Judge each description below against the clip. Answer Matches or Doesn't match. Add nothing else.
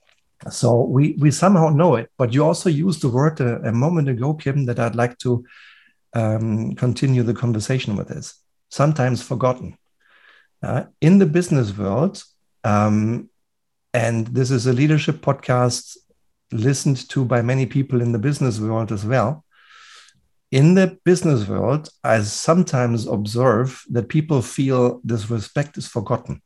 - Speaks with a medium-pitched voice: Doesn't match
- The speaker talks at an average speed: Matches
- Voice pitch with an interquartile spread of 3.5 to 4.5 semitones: Matches